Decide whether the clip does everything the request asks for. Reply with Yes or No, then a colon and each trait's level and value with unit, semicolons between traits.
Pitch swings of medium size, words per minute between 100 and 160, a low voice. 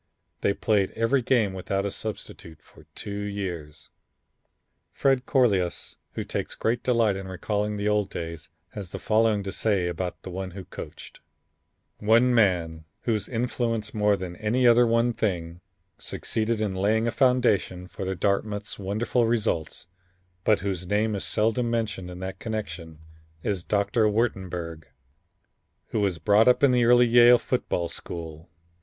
Yes: average, 3.6 semitones; average, 150 wpm; low, 105 Hz